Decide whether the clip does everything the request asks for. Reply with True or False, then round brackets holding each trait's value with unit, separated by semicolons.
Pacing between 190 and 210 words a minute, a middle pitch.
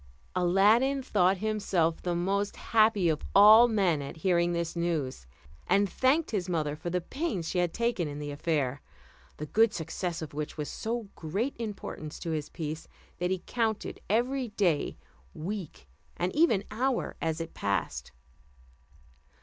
False (160 wpm; 180 Hz)